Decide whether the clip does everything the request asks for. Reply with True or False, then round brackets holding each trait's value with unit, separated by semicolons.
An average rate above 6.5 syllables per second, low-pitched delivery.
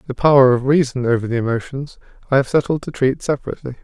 True (7.0 syllables/s; 130 Hz)